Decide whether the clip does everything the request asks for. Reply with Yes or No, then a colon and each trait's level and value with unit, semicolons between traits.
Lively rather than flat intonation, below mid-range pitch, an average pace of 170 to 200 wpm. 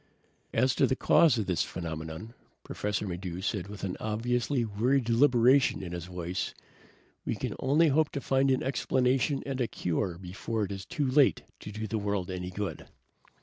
Yes: wide, 5.9 semitones; low, 110 Hz; average, 180 wpm